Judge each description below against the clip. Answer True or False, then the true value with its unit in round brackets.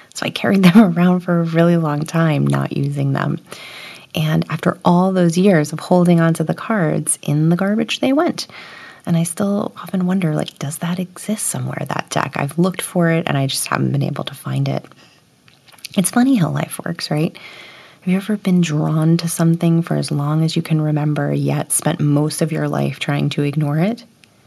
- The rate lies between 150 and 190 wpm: False (205 wpm)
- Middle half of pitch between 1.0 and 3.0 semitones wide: False (3.4 semitones)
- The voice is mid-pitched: True (165 Hz)